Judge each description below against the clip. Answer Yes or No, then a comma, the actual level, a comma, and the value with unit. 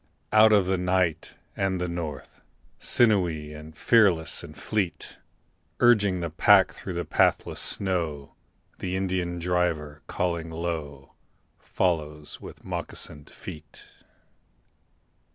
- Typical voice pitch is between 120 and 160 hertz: No, very low, 85 Hz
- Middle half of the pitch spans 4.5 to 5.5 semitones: No, average, 3.2 semitones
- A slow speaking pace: Yes, slow, 105 wpm